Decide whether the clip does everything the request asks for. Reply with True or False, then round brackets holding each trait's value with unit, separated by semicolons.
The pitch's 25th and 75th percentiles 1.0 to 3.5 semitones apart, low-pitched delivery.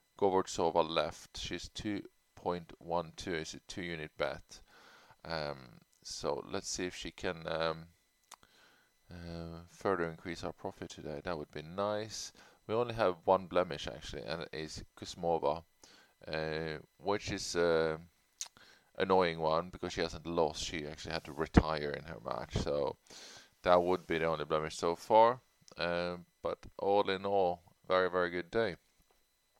True (2.4 semitones; 85 Hz)